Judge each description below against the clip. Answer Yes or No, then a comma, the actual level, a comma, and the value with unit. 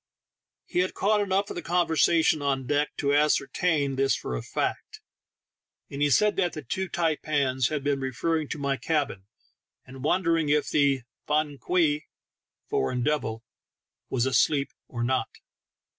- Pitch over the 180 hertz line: No, medium, 145 Hz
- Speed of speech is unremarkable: Yes, average, 160 wpm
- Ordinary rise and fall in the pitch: Yes, average, 3.4 semitones